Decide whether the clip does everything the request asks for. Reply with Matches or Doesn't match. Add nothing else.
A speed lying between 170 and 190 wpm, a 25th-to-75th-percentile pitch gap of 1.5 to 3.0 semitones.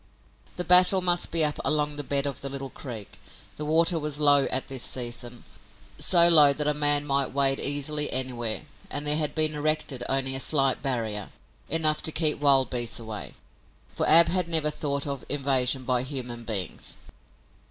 Matches